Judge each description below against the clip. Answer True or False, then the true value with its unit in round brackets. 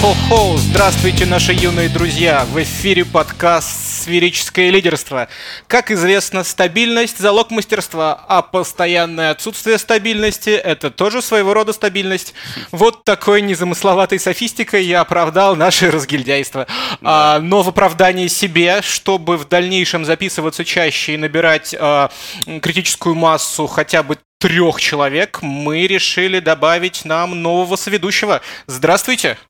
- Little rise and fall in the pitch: False (3.7 semitones)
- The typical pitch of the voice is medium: True (180 Hz)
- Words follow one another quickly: False (115 wpm)